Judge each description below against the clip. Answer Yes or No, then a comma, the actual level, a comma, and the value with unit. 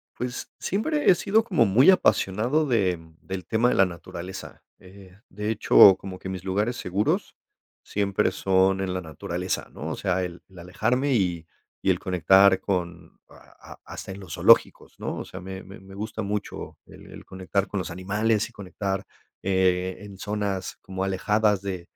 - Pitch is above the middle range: No, very low, 95 Hz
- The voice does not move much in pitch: Yes, narrow, 2.2 semitones